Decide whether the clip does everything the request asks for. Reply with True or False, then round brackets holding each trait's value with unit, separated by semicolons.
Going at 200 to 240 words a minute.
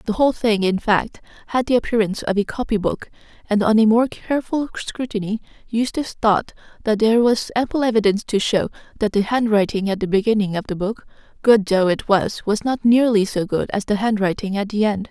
True (205 wpm)